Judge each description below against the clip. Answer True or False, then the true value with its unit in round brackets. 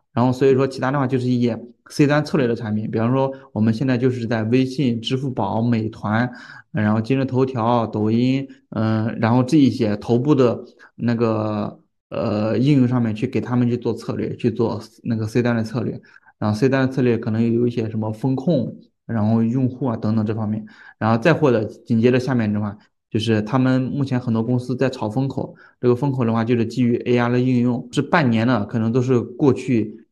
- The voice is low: True (120 Hz)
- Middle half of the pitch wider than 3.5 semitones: False (2.5 semitones)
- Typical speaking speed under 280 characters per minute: False (310 characters per minute)